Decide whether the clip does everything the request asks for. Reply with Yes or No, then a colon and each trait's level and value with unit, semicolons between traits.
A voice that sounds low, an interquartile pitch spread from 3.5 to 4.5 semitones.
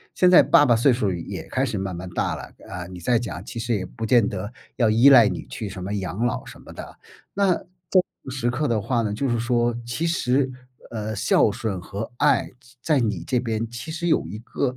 Yes: low, 115 Hz; average, 3.8 semitones